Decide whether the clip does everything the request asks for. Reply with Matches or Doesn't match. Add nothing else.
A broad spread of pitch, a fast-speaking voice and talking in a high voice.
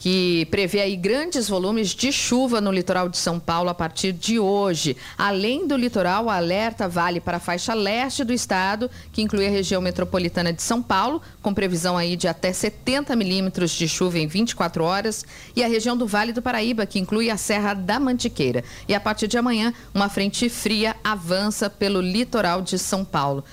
Doesn't match